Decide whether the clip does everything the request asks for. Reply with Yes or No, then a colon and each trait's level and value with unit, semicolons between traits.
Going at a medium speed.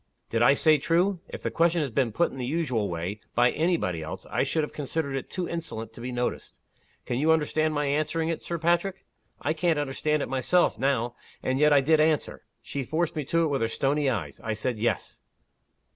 No: fast, 220 wpm